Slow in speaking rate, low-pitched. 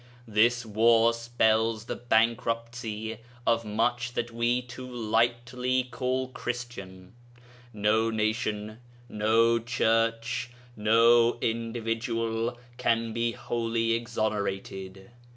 Yes: slow, 90 wpm; low, 115 Hz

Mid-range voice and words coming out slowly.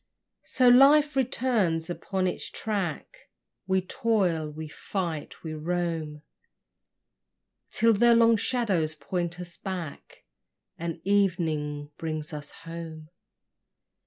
Yes: medium, 175 Hz; slow, 100 wpm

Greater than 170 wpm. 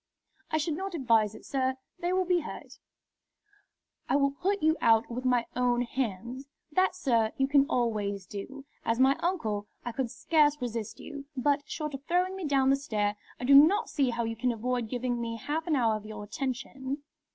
Yes: average, 195 wpm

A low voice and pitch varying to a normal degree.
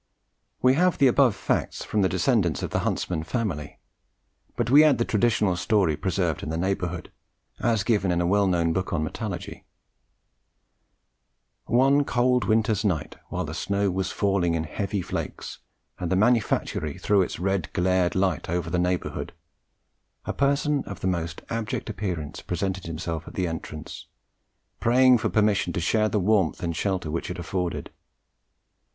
Yes: very low, 95 Hz; average, 4.1 semitones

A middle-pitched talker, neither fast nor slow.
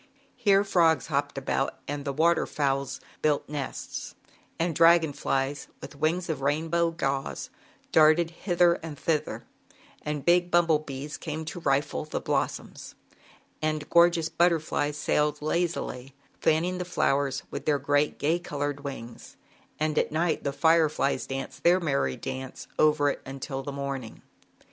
Yes: medium, 150 Hz; average, 145 wpm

